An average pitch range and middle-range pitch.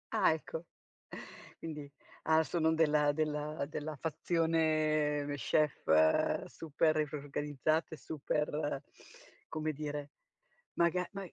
No: narrow, 1.4 semitones; medium, 155 Hz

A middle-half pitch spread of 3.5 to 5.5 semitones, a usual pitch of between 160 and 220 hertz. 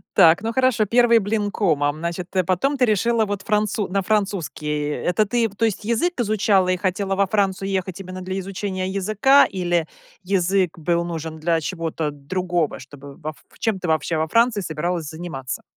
Yes: average, 4.1 semitones; medium, 185 Hz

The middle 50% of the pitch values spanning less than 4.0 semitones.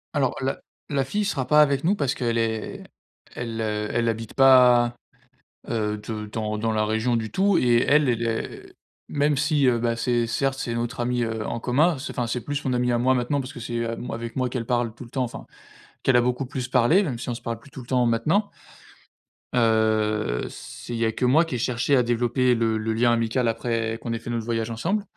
Yes: narrow, 2.4 semitones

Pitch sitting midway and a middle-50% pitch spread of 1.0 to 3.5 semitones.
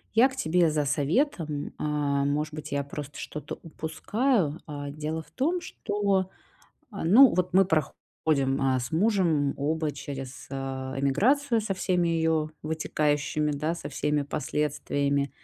No: medium, 155 Hz; average, 4.2 semitones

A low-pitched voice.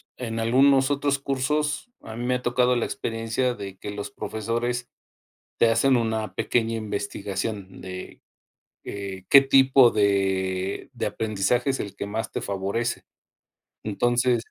Yes: low, 115 Hz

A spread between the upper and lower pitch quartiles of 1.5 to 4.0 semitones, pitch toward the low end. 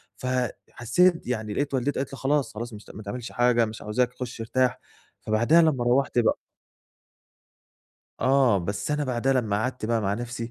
Yes: average, 3.1 semitones; low, 120 Hz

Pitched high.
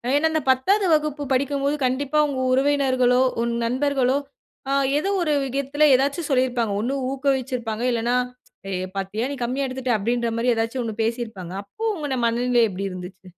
Yes: very high, 255 Hz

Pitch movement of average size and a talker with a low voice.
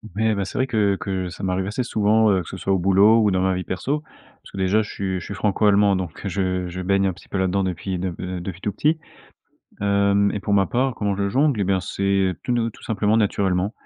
No: narrow, 2.1 semitones; low, 100 Hz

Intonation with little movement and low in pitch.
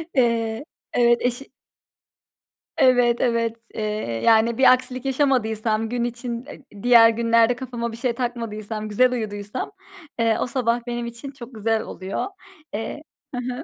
No: narrow, 1.8 semitones; high, 235 Hz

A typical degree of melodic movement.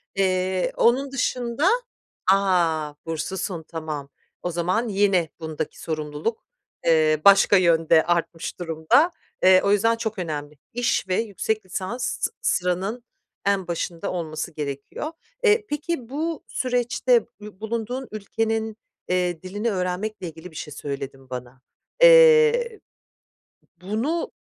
No: wide, 6.0 semitones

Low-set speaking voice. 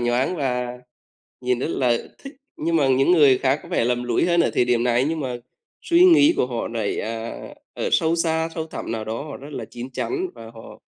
Yes: low, 130 Hz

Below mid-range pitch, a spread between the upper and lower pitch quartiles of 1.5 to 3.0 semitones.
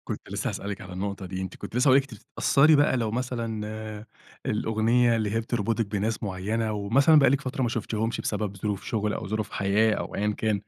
Yes: low, 110 Hz; narrow, 2.4 semitones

